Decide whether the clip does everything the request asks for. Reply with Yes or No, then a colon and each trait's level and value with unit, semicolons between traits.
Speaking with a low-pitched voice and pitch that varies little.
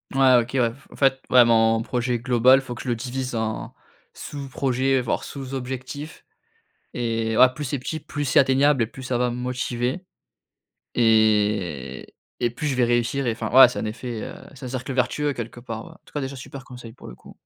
Yes: low, 125 Hz; narrow, 2.2 semitones